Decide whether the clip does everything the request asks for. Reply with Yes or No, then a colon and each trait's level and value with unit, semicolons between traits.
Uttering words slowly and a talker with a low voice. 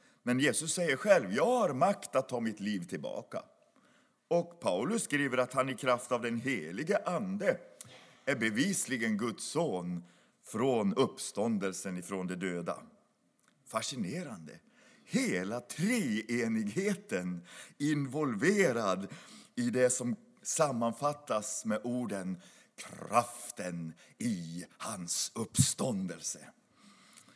Yes: slow, 100 wpm; low, 120 Hz